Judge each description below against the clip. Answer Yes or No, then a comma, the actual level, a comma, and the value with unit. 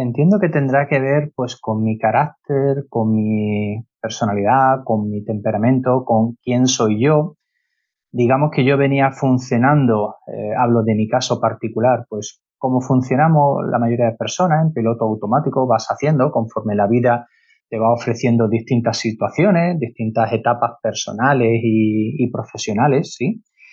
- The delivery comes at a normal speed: Yes, average, 145 wpm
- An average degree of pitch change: Yes, average, 3.5 semitones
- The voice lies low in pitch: Yes, low, 120 Hz